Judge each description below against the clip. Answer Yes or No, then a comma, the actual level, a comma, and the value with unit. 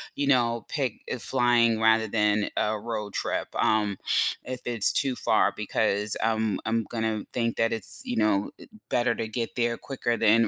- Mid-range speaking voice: No, low, 115 Hz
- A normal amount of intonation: No, narrow, 1.8 semitones